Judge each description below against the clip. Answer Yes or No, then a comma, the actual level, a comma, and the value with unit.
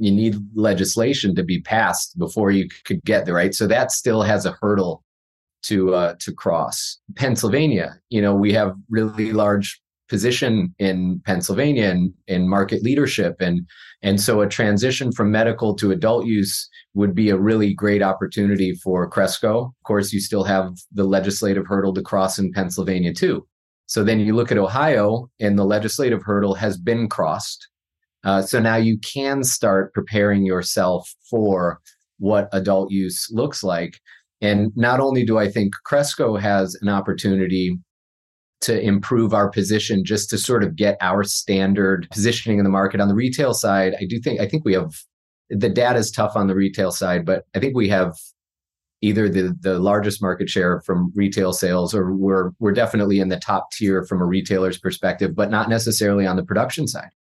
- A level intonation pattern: Yes, narrow, 2.3 semitones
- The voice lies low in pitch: Yes, low, 100 Hz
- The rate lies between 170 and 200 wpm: Yes, average, 180 wpm